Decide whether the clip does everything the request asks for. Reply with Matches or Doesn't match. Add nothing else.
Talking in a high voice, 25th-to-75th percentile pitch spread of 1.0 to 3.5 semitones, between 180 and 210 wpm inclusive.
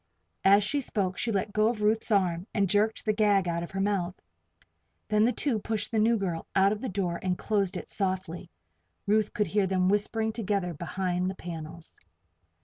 Matches